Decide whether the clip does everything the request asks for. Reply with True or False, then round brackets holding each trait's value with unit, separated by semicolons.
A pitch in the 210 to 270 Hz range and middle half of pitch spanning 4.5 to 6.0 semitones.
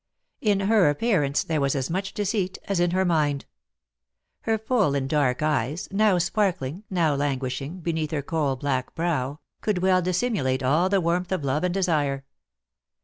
False (165 Hz; 5.1 semitones)